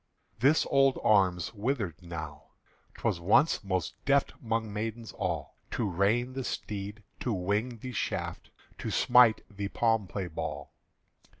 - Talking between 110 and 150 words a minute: Yes, average, 140 wpm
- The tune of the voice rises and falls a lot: No, average, 4.4 semitones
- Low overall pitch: Yes, low, 105 Hz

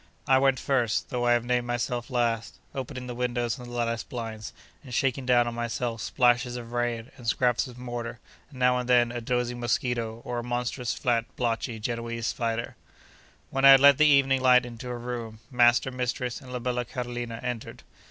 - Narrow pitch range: Yes, narrow, 1.1 semitones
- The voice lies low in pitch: Yes, low, 120 Hz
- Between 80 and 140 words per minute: No, average, 195 wpm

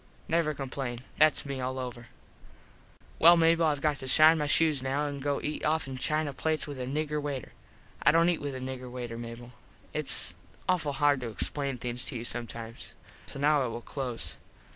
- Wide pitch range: No, average, 3.3 semitones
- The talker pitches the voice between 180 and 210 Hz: No, medium, 140 Hz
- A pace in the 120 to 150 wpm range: No, average, 195 wpm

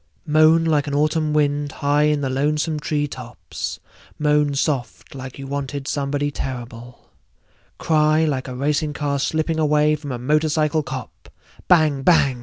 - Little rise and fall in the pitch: Yes, narrow, 1.8 semitones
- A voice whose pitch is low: No, medium, 145 Hz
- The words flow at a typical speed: Yes, average, 150 wpm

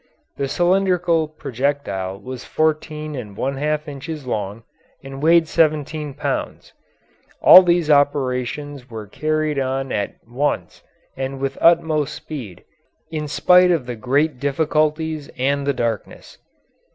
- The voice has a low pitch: No, medium, 145 Hz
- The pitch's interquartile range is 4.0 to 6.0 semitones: No, average, 3.1 semitones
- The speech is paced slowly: Yes, slow, 125 wpm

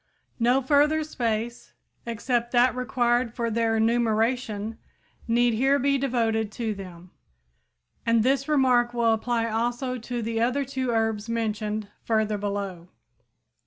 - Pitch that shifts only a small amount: Yes, narrow, 2.2 semitones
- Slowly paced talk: Yes, slow, 125 wpm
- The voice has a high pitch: Yes, high, 235 Hz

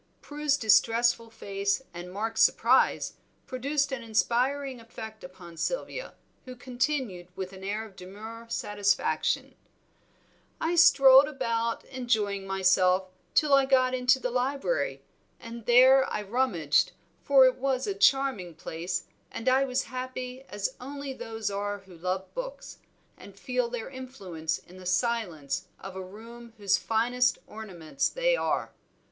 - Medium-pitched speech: No, high, 230 Hz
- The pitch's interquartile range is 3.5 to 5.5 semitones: Yes, average, 5.1 semitones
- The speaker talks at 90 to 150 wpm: Yes, average, 140 wpm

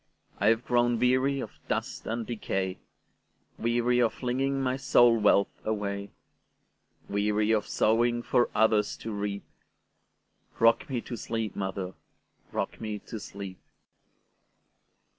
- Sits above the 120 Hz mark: No, low, 115 Hz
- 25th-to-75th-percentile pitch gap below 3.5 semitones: Yes, average, 2.8 semitones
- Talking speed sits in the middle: No, slow, 105 wpm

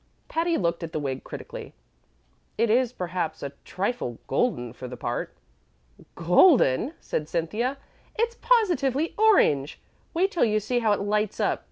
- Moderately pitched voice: No, high, 215 Hz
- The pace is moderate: Yes, average, 150 wpm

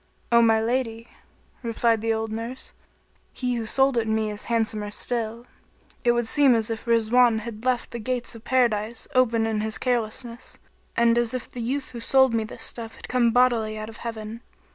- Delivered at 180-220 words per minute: Yes, average, 190 wpm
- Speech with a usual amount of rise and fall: No, narrow, 1.7 semitones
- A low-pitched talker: No, high, 230 Hz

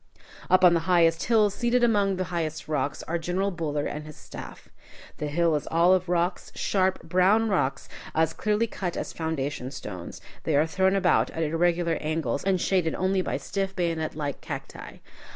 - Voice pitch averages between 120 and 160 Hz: No, medium, 170 Hz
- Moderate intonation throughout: Yes, average, 3.2 semitones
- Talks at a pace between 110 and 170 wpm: No, average, 185 wpm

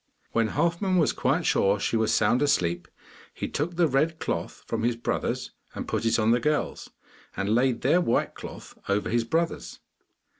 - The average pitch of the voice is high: No, low, 120 Hz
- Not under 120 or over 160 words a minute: No, average, 180 wpm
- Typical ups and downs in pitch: No, wide, 6.3 semitones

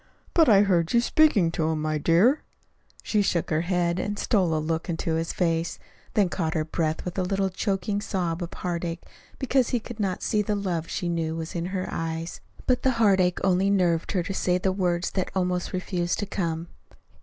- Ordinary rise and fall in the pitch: Yes, average, 3.0 semitones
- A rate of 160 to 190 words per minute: No, fast, 205 wpm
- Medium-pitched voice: Yes, medium, 180 Hz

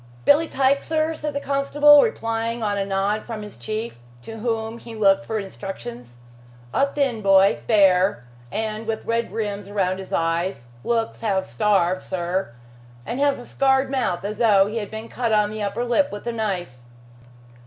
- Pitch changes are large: No, average, 3.5 semitones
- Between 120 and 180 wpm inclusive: Yes, average, 175 wpm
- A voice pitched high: Yes, high, 215 Hz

